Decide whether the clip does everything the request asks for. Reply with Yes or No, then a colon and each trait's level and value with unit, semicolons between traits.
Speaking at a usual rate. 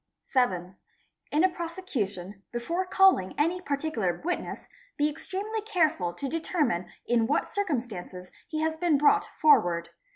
No: slow, 130 wpm